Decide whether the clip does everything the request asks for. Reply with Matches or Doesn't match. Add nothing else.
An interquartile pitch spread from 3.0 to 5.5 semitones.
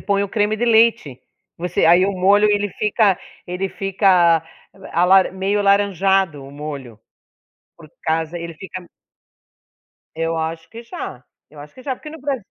Matches